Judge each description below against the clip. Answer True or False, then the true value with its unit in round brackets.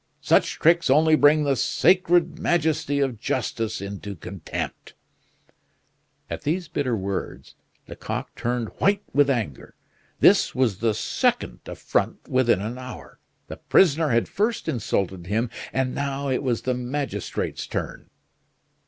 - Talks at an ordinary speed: False (130 wpm)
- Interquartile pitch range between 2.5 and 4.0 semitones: False (5.2 semitones)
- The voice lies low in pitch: True (130 Hz)